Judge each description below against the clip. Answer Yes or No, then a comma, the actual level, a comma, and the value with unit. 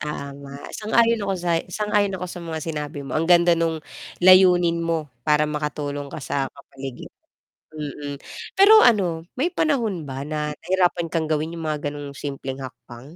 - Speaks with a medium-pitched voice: Yes, medium, 160 Hz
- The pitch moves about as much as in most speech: Yes, average, 3.8 semitones